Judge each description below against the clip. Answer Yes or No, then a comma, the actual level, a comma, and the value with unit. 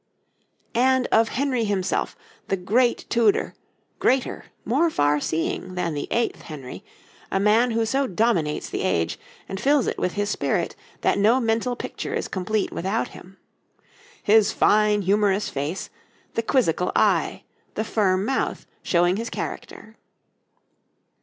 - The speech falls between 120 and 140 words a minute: Yes, slow, 135 wpm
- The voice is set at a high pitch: Yes, high, 210 Hz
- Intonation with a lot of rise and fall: No, average, 4.2 semitones